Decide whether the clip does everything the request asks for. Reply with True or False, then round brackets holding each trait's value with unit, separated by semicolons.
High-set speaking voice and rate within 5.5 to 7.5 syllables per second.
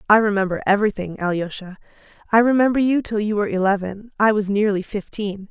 True (205 Hz; 6.2 syllables/s)